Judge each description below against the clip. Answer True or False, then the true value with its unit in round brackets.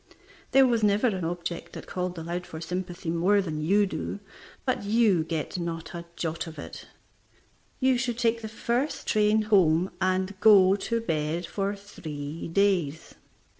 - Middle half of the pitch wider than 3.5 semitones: True (4.1 semitones)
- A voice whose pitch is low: False (185 Hz)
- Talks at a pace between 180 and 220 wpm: False (160 wpm)